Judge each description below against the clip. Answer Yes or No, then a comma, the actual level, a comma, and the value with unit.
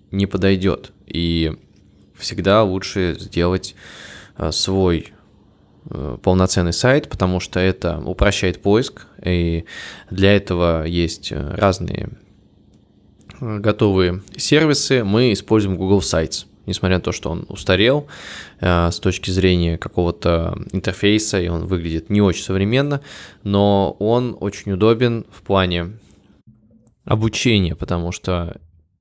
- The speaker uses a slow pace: Yes, slow, 105 wpm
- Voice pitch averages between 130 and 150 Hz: No, very low, 95 Hz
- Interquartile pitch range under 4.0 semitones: Yes, average, 2.9 semitones